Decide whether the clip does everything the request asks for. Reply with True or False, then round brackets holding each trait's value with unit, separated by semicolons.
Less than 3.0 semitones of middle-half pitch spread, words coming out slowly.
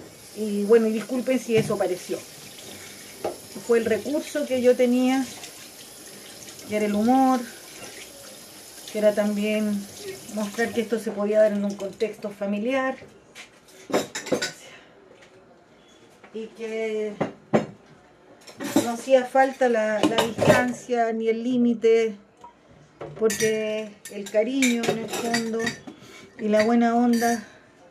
True (2.5 semitones; 110 wpm)